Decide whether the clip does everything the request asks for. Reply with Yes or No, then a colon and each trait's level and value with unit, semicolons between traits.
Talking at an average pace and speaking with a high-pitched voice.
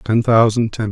No: average, 195 wpm; low, 110 Hz